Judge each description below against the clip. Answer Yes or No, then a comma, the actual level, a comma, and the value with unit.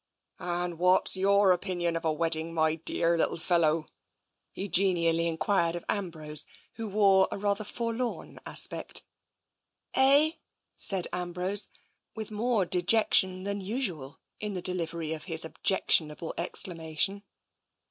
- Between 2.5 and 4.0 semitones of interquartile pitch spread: Yes, average, 3.3 semitones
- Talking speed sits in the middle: No, slow, 130 wpm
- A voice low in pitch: No, medium, 180 Hz